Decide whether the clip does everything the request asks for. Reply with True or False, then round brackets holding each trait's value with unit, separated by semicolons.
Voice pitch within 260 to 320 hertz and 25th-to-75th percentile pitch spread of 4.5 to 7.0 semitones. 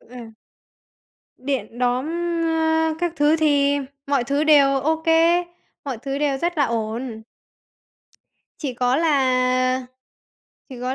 False (275 Hz; 3.0 semitones)